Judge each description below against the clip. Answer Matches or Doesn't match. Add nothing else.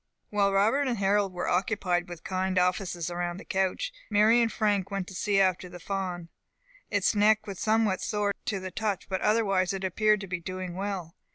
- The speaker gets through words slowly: Doesn't match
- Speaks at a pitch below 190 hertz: Doesn't match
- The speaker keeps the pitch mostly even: Matches